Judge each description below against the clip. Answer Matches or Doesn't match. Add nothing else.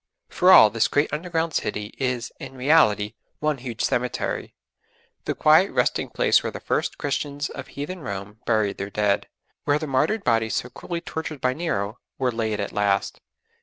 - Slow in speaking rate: Doesn't match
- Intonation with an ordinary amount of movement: Doesn't match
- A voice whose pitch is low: Matches